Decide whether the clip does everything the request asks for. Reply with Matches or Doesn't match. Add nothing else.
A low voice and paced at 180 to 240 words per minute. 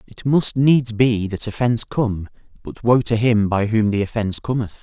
Matches